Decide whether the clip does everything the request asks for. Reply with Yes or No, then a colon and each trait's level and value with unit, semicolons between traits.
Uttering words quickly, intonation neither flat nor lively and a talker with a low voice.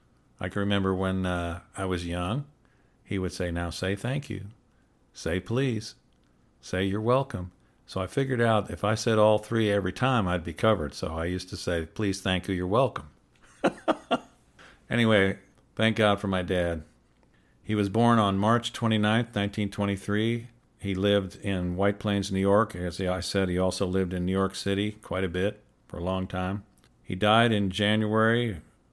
No: average, 180 wpm; average, 3.0 semitones; low, 100 Hz